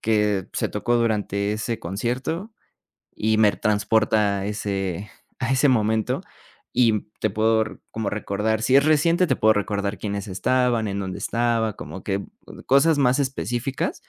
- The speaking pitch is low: Yes, low, 110 Hz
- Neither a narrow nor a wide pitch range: Yes, average, 3.3 semitones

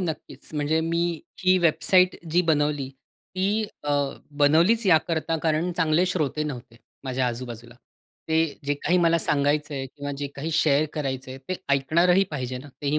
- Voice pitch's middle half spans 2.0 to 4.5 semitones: Yes, average, 3.3 semitones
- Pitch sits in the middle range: Yes, medium, 155 Hz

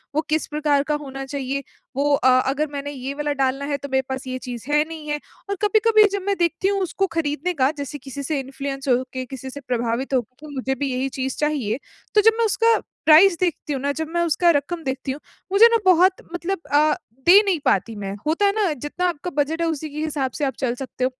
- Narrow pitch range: No, average, 4.1 semitones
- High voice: Yes, very high, 290 Hz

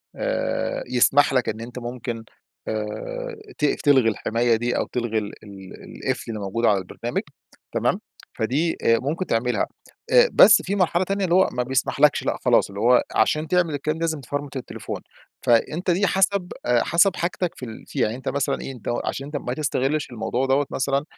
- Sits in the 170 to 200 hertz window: No, low, 135 Hz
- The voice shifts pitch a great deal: Yes, wide, 6.1 semitones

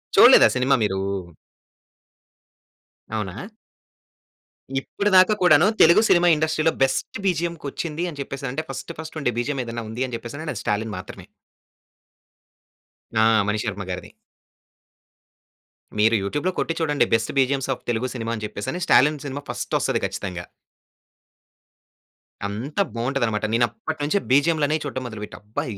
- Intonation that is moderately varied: No, wide, 5.7 semitones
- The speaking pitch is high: No, low, 135 Hz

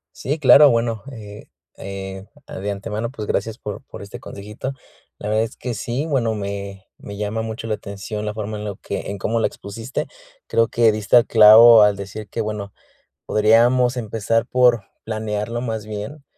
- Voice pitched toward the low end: Yes, low, 110 Hz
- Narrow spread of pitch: Yes, narrow, 2.1 semitones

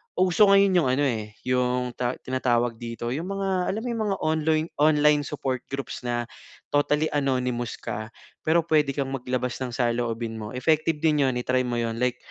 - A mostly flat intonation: No, average, 4.3 semitones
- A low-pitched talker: Yes, low, 130 Hz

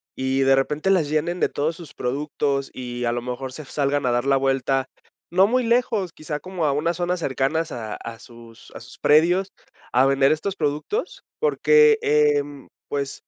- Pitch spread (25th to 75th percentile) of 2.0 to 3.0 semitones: No, average, 4.4 semitones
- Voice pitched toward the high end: No, medium, 145 Hz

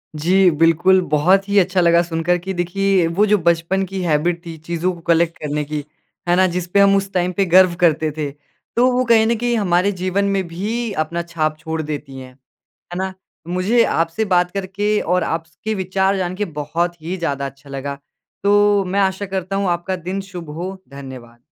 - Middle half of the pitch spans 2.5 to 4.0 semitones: Yes, average, 3.0 semitones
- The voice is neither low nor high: Yes, medium, 180 Hz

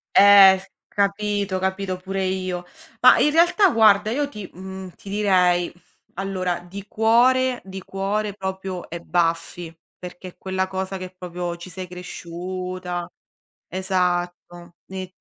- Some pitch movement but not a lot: No, narrow, 1.9 semitones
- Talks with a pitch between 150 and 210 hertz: Yes, high, 190 Hz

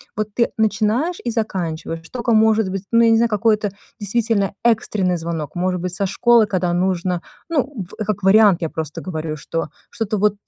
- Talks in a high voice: Yes, high, 205 Hz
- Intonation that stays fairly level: No, average, 4.0 semitones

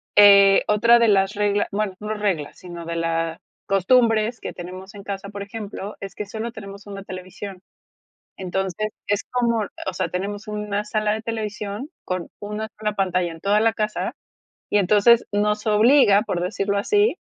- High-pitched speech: Yes, high, 205 Hz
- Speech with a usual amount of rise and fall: No, narrow, 1.8 semitones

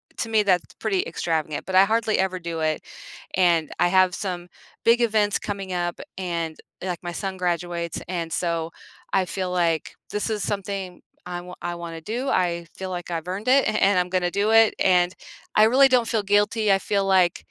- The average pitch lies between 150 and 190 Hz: Yes, medium, 185 Hz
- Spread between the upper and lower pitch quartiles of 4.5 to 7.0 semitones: No, average, 2.9 semitones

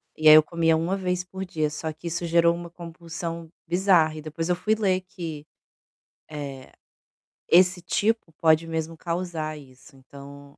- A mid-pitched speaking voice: Yes, medium, 165 Hz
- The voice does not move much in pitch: Yes, narrow, 2.3 semitones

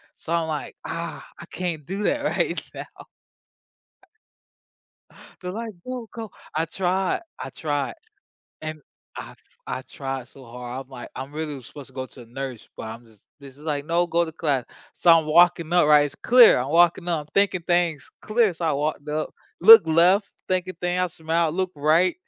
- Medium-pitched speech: Yes, medium, 160 Hz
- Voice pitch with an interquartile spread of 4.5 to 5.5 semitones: No, average, 4.1 semitones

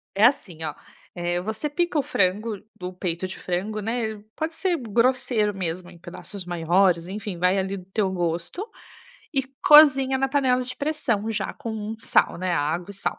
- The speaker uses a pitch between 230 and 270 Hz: No, high, 205 Hz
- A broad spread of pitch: Yes, wide, 5.8 semitones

